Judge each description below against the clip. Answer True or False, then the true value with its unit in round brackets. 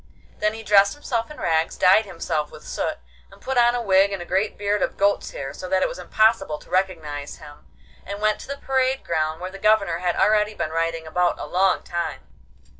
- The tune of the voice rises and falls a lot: False (4.4 semitones)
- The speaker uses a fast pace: True (220 wpm)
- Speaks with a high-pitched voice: True (195 Hz)